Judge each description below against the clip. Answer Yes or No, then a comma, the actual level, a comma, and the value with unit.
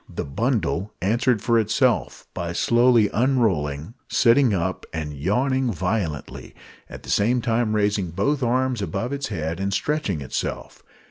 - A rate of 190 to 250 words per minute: No, average, 140 wpm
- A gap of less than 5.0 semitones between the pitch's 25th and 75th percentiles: No, wide, 5.4 semitones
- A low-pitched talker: Yes, low, 110 Hz